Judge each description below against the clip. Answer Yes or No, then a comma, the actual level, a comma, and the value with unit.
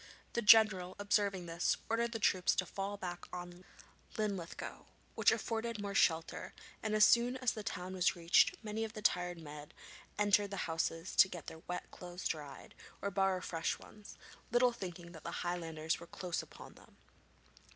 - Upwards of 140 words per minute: Yes, average, 170 wpm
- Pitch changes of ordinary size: Yes, average, 3.3 semitones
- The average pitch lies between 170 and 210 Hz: Yes, medium, 185 Hz